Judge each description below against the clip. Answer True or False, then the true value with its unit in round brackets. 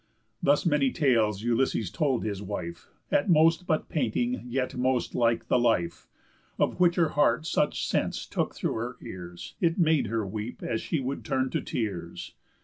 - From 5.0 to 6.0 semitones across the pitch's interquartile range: True (5.5 semitones)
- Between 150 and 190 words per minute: True (170 wpm)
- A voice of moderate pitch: False (125 Hz)